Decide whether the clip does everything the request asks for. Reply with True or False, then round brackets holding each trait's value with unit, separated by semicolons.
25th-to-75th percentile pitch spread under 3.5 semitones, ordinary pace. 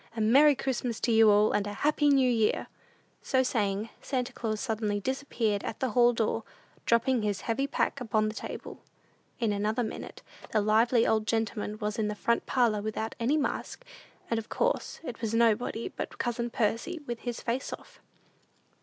True (2.6 semitones; 180 wpm)